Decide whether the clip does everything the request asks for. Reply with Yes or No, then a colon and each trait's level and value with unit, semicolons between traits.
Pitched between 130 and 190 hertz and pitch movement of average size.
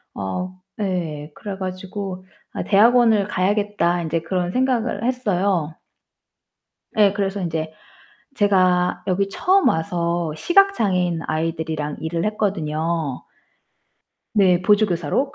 Yes: medium, 185 Hz; average, 3.7 semitones